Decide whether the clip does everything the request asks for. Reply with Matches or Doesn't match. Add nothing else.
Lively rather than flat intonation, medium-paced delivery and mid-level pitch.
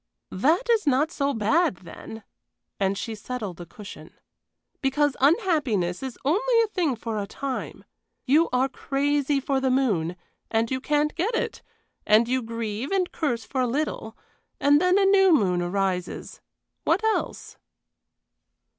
Doesn't match